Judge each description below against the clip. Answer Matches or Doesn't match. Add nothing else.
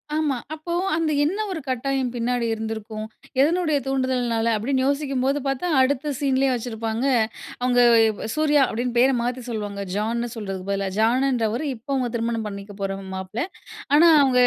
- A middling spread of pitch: Matches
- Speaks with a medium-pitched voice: Doesn't match